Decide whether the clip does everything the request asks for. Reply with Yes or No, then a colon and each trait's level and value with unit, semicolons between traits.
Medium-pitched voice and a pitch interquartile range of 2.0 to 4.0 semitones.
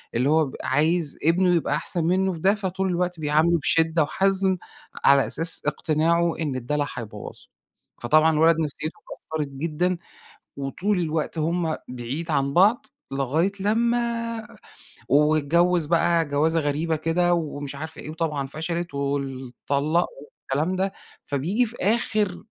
Yes: medium, 160 Hz; average, 3.5 semitones